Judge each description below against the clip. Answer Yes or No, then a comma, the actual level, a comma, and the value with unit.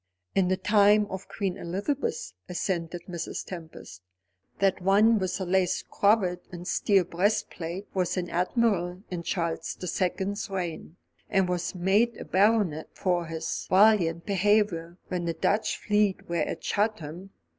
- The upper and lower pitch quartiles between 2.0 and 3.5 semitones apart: Yes, average, 2.8 semitones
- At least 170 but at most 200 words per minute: No, average, 145 wpm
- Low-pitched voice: No, medium, 185 Hz